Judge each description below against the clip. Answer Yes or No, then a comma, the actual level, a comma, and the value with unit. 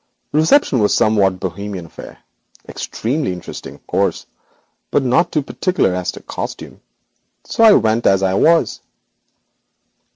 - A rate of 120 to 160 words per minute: Yes, average, 140 wpm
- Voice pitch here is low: Yes, low, 110 Hz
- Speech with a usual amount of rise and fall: No, wide, 8.4 semitones